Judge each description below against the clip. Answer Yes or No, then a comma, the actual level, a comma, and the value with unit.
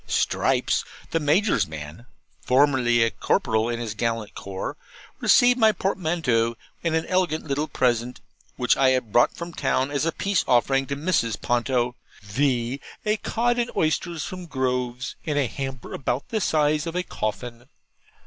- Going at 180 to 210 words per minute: No, average, 155 wpm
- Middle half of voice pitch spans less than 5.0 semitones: No, wide, 5.4 semitones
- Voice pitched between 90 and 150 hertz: Yes, low, 135 Hz